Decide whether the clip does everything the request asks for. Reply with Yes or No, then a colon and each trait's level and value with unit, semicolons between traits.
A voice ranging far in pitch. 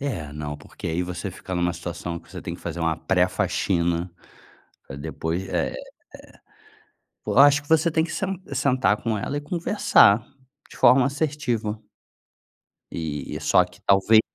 Yes: wide, 8.7 semitones